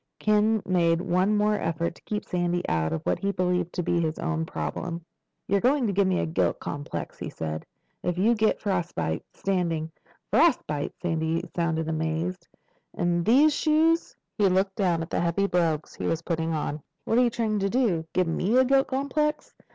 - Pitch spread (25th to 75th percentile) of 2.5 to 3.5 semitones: No, average, 4.5 semitones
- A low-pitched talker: No, medium, 180 Hz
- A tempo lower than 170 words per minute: No, average, 190 wpm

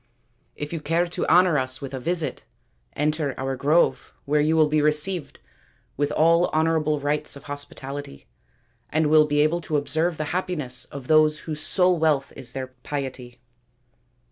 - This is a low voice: No, medium, 150 Hz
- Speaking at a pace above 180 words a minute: No, average, 165 wpm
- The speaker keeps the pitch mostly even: Yes, narrow, 2.3 semitones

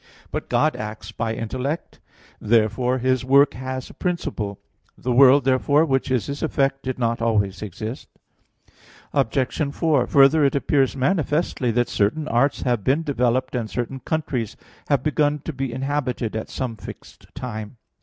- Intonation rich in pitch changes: No, average, 3.3 semitones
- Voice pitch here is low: Yes, low, 130 Hz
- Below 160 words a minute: Yes, average, 150 wpm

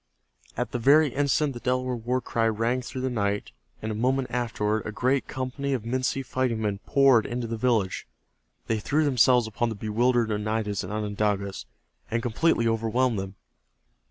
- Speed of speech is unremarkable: Yes, average, 170 wpm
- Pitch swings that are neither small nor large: Yes, average, 3.0 semitones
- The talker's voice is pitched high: No, low, 115 Hz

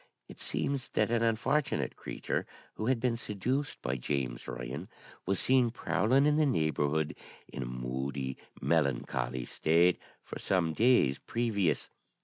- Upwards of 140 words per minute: No, slow, 135 wpm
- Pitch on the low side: Yes, very low, 90 Hz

